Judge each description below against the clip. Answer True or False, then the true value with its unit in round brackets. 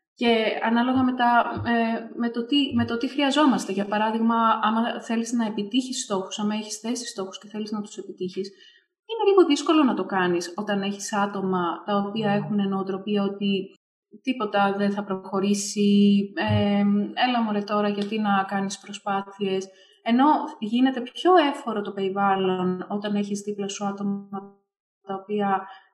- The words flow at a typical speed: True (155 wpm)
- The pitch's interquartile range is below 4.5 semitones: True (3.0 semitones)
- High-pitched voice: True (205 Hz)